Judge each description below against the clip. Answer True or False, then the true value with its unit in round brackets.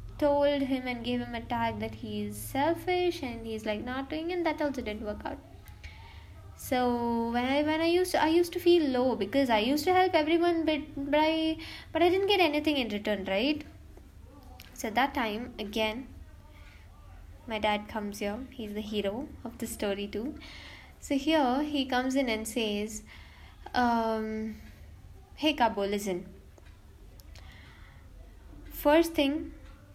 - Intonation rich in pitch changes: True (6.9 semitones)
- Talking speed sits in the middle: True (160 wpm)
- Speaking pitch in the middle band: False (235 Hz)